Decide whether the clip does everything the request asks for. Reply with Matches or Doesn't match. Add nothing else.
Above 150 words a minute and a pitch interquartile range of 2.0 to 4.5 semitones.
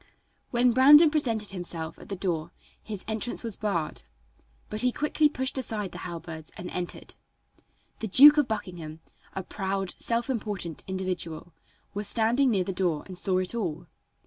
Doesn't match